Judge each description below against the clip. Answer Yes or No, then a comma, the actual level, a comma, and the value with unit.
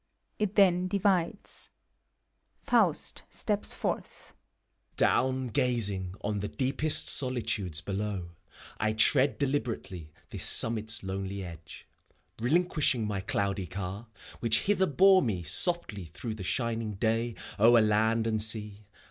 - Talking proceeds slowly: Yes, slow, 120 wpm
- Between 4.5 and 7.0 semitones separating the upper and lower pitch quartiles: Yes, average, 4.9 semitones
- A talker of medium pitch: No, low, 110 Hz